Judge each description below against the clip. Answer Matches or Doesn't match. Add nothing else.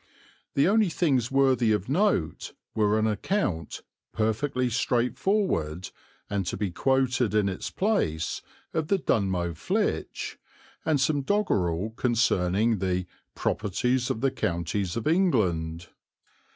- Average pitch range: Doesn't match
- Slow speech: Matches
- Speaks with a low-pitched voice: Matches